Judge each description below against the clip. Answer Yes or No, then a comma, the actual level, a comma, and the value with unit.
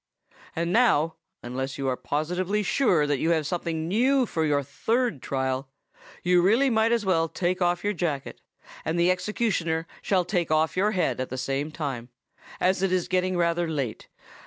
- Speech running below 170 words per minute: No, average, 180 wpm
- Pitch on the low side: No, medium, 170 Hz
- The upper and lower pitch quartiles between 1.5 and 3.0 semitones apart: No, average, 4.3 semitones